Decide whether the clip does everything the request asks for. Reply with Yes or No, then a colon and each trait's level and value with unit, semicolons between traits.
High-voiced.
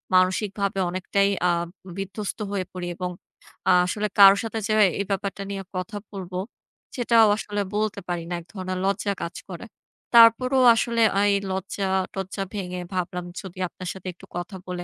Yes: high, 195 Hz